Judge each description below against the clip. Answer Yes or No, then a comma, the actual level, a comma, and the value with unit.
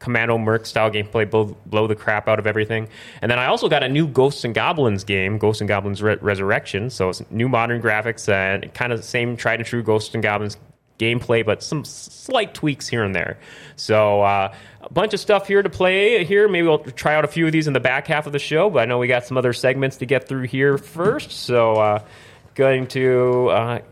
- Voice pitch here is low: Yes, low, 120 Hz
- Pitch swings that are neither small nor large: Yes, average, 4.4 semitones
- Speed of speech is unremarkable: No, fast, 235 wpm